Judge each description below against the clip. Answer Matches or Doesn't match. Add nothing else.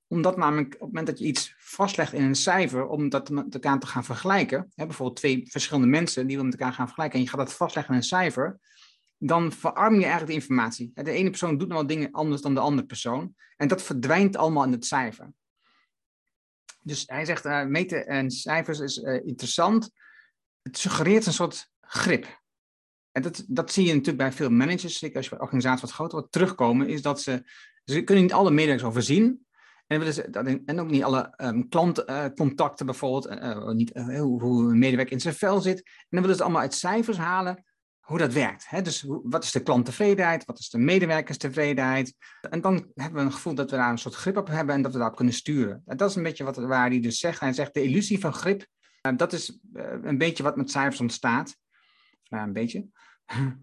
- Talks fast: Matches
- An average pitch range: Matches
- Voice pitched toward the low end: Doesn't match